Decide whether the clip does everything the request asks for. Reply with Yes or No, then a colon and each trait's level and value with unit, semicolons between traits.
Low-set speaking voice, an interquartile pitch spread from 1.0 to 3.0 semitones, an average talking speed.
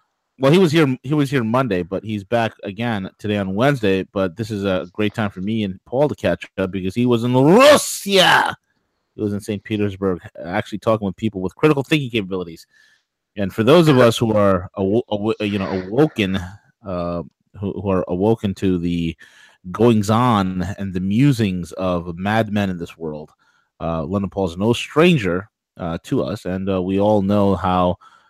No: low, 100 Hz; average, 3.7 semitones; average, 190 wpm